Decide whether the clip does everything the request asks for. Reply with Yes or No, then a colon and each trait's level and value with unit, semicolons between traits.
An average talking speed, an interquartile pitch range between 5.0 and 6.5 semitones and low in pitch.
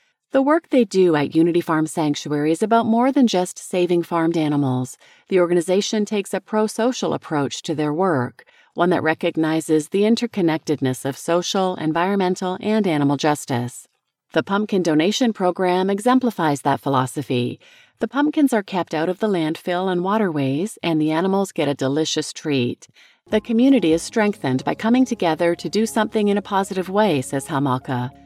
No: average, 160 wpm; wide, 5.4 semitones; medium, 175 Hz